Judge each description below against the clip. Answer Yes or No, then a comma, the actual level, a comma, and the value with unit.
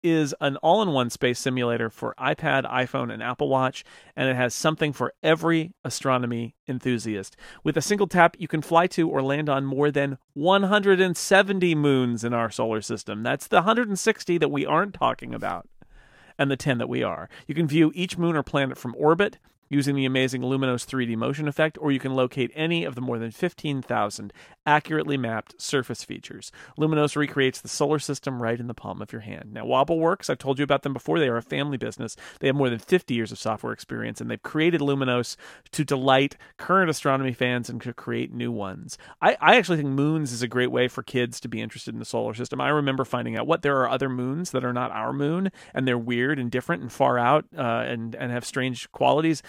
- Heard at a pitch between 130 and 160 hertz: Yes, low, 135 Hz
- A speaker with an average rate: No, fast, 215 wpm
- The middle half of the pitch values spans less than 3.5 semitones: No, average, 4.0 semitones